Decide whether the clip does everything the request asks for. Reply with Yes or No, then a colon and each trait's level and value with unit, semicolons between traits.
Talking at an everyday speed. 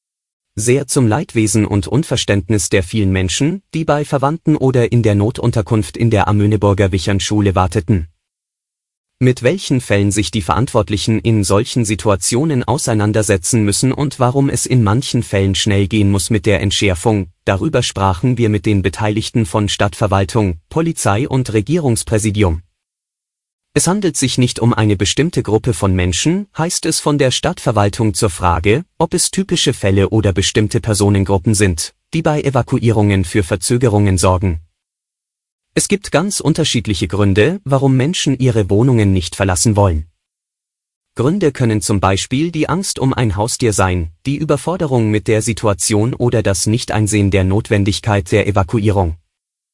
Yes: average, 145 wpm